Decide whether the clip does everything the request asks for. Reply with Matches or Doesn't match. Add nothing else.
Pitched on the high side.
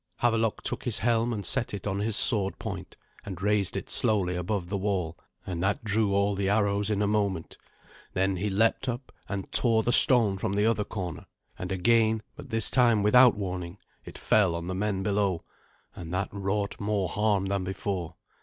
Doesn't match